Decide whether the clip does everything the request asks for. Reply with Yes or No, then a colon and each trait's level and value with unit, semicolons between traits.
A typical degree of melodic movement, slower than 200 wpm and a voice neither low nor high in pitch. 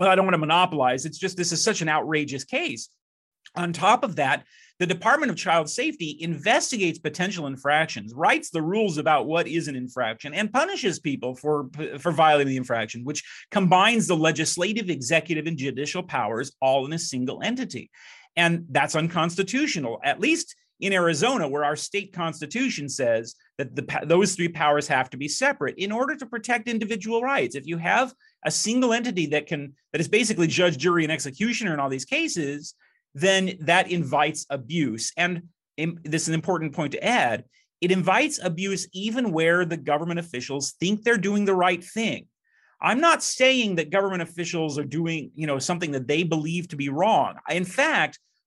Yes: average, 4.7 semitones; average, 180 wpm; medium, 170 Hz